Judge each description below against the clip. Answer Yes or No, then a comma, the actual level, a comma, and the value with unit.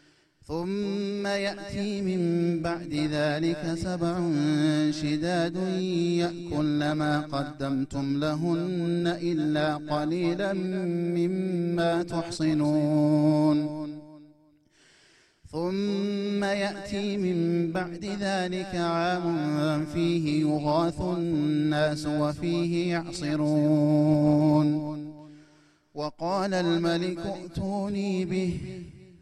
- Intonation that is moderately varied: Yes, average, 3.0 semitones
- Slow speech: Yes, slow, 60 wpm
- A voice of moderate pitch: Yes, medium, 170 Hz